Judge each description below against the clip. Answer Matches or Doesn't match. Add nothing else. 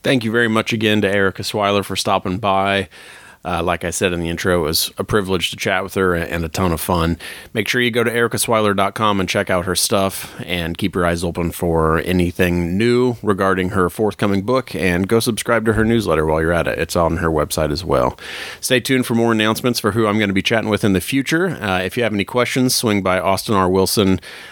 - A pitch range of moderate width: Matches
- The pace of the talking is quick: Matches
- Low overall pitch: Matches